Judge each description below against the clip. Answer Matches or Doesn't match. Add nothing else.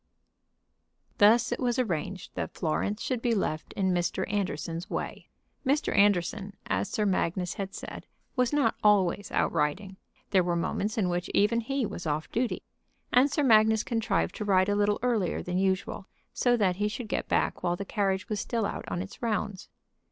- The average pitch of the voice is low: Doesn't match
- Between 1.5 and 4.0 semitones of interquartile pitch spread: Matches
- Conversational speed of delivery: Matches